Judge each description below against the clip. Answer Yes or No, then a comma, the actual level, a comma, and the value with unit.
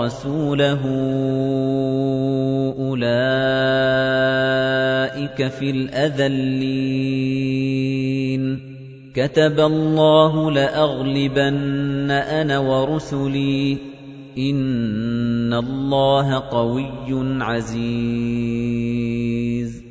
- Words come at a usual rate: No, slow, 40 wpm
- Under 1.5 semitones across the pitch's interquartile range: Yes, narrow, 0.8 semitones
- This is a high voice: No, low, 135 Hz